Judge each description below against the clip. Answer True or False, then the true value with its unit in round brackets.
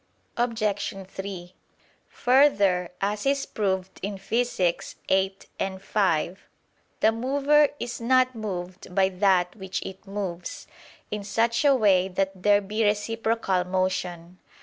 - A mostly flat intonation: False (3.4 semitones)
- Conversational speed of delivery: False (120 wpm)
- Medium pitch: False (195 Hz)